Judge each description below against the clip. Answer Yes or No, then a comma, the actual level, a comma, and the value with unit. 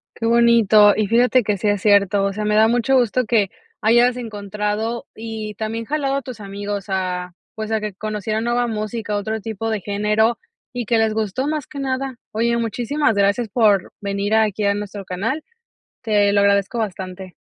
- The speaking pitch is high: Yes, high, 215 Hz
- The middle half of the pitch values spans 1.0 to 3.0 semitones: Yes, narrow, 2.5 semitones